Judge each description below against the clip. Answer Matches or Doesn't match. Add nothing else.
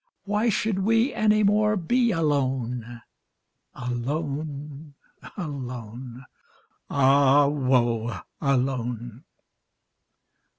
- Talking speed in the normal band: Doesn't match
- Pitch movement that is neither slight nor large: Doesn't match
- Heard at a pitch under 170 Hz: Matches